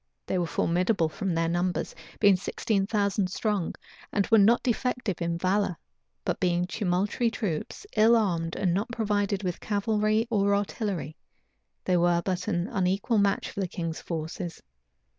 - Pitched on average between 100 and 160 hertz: No, high, 195 Hz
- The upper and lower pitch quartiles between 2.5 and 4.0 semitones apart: Yes, average, 3.2 semitones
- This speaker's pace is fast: No, average, 155 wpm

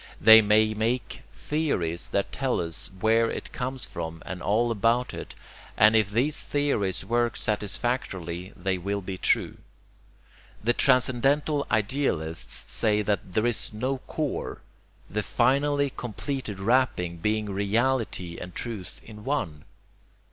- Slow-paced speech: Yes, slow, 125 wpm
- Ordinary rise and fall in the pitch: Yes, average, 4.7 semitones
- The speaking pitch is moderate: No, low, 110 Hz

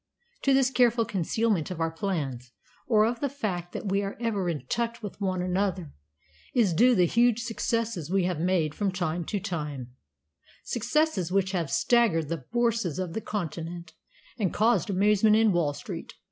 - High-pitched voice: Yes, high, 195 Hz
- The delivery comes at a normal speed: Yes, average, 175 wpm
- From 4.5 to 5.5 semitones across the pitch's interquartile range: Yes, average, 5.2 semitones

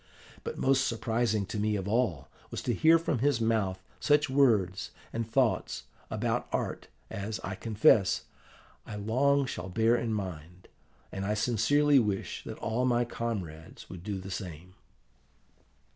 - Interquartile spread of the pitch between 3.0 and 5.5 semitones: Yes, average, 4.1 semitones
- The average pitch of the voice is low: Yes, low, 110 Hz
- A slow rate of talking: No, average, 150 wpm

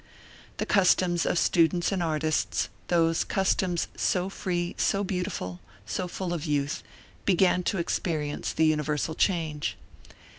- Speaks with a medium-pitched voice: Yes, medium, 175 Hz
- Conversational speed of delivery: No, slow, 125 wpm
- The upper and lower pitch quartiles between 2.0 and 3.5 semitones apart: Yes, average, 2.8 semitones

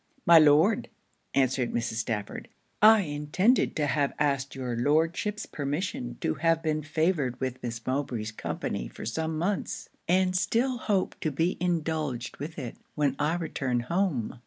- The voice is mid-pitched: Yes, medium, 150 Hz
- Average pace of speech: Yes, average, 150 wpm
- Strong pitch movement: No, average, 4.8 semitones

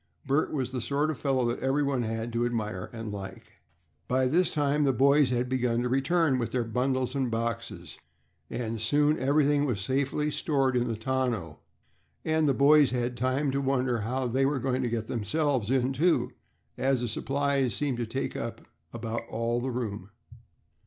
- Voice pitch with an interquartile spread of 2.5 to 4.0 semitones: Yes, average, 3.0 semitones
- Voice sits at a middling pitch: No, low, 130 Hz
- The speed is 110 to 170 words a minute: No, average, 180 wpm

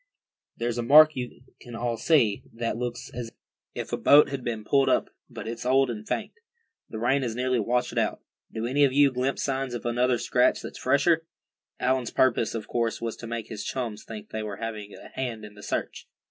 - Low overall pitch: Yes, low, 120 Hz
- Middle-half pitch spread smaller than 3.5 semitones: Yes, narrow, 2.6 semitones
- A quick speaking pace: Yes, fast, 215 wpm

